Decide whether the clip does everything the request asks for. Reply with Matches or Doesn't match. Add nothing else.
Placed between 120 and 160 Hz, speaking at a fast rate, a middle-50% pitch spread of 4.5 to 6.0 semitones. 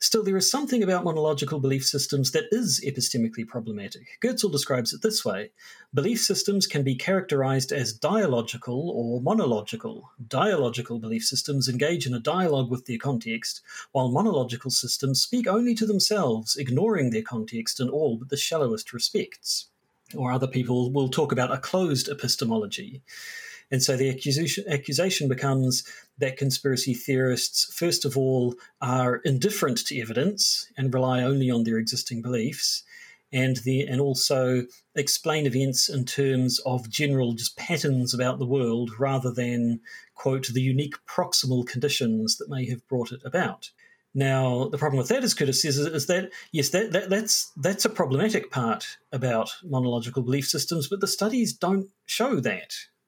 Doesn't match